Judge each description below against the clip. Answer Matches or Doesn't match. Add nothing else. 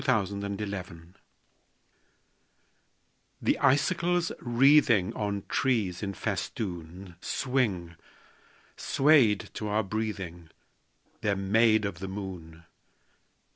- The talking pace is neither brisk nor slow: Doesn't match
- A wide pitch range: Doesn't match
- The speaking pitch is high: Doesn't match